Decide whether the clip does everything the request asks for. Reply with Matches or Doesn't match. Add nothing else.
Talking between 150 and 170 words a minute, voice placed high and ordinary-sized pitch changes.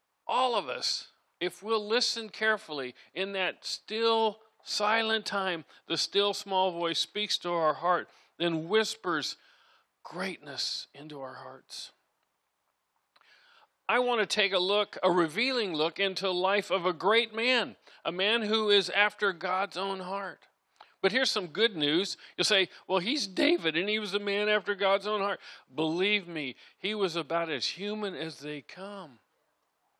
Matches